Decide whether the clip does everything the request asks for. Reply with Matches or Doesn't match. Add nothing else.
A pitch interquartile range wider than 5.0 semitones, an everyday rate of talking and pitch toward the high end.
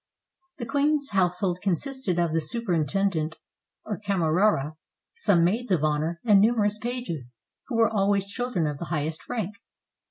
Matches